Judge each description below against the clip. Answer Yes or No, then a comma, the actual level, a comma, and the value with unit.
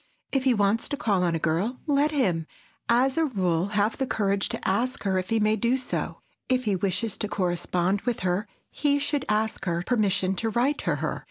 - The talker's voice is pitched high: Yes, high, 210 Hz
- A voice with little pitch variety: No, average, 5.2 semitones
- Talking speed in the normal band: No, fast, 210 wpm